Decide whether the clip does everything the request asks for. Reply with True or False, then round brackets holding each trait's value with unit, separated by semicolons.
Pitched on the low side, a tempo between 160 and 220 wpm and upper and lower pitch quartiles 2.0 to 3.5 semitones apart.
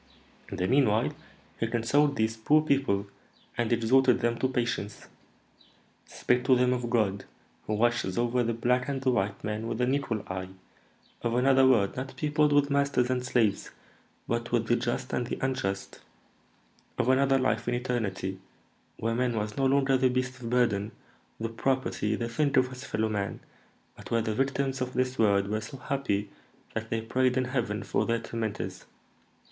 True (120 Hz; 175 wpm; 3.0 semitones)